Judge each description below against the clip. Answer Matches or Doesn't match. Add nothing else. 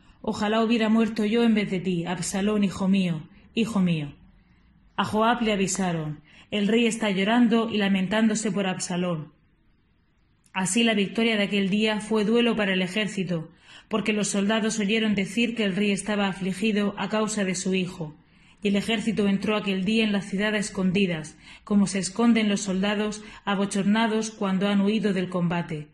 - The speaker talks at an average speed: Matches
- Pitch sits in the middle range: Doesn't match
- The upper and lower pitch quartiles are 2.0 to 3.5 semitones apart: Matches